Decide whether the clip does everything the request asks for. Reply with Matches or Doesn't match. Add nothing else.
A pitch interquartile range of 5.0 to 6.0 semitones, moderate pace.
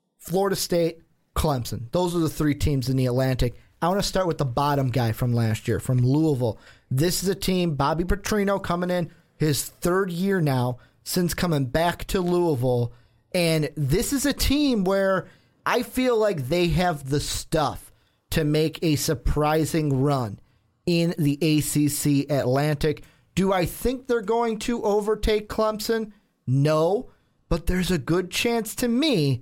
Matches